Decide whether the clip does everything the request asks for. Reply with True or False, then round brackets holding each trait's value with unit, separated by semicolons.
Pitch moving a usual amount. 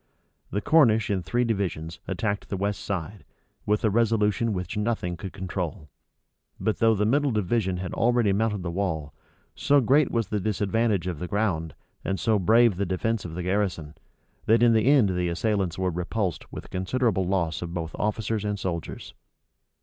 True (3.9 semitones)